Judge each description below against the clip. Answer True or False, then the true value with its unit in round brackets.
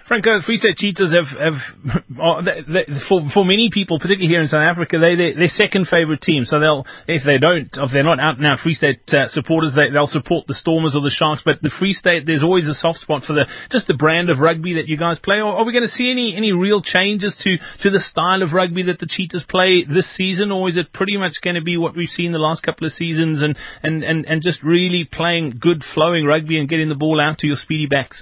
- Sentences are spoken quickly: True (265 wpm)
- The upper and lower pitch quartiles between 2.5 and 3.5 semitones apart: True (3.1 semitones)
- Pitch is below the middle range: False (165 Hz)